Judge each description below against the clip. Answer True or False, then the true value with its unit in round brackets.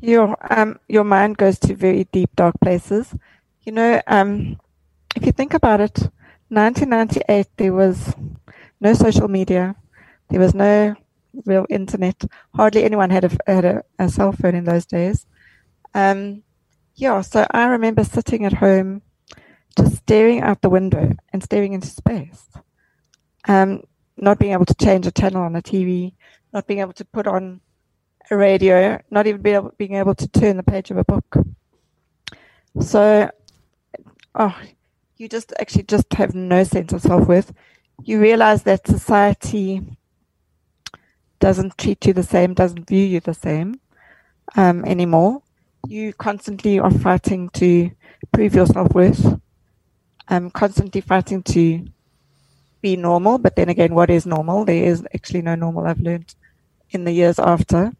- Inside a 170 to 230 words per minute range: False (155 wpm)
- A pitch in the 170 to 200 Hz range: True (190 Hz)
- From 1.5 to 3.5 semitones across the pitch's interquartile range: True (2.8 semitones)